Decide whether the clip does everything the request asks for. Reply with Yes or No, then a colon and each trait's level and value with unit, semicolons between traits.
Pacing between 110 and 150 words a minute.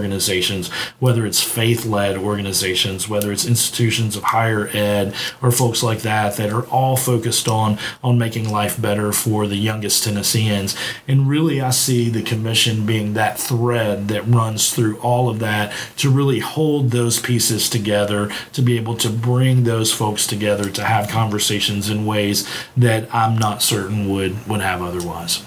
No: average, 165 wpm